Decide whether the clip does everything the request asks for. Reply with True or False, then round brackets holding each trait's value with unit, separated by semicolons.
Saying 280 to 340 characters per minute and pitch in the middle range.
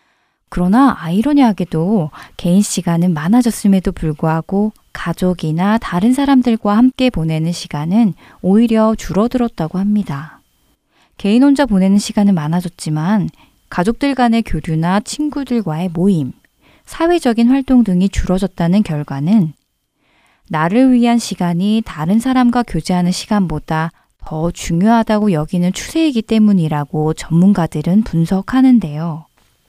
False (305 characters per minute; 195 Hz)